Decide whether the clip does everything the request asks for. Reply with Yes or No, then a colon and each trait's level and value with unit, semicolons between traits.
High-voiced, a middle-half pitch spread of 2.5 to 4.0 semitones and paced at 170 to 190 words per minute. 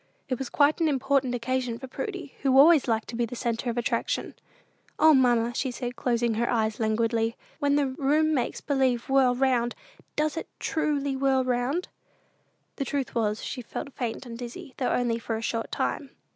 Yes: very high, 255 Hz; average, 2.9 semitones; average, 185 wpm